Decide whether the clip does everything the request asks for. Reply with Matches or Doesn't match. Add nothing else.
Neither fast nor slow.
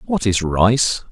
Matches